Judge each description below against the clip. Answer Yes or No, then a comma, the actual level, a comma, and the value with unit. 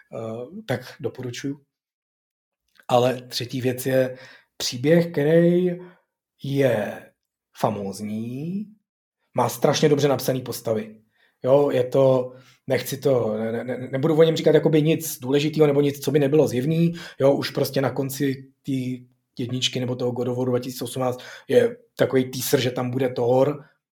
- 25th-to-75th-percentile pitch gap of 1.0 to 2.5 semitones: No, average, 2.9 semitones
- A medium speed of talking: Yes, average, 135 wpm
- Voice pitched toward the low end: Yes, low, 130 Hz